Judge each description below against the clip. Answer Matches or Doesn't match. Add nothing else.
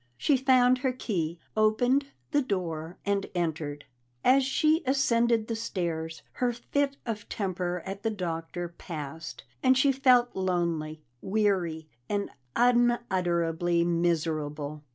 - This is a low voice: Doesn't match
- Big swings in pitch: Matches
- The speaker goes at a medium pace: Doesn't match